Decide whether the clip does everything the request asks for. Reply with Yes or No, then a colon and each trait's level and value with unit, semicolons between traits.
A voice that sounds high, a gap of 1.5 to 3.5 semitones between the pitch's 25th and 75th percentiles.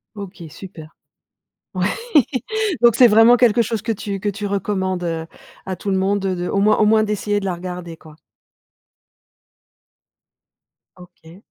Yes: high, 195 Hz; average, 2.9 semitones